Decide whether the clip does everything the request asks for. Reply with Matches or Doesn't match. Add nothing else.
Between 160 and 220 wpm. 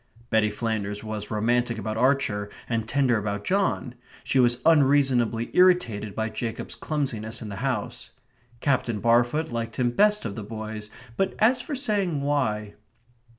Doesn't match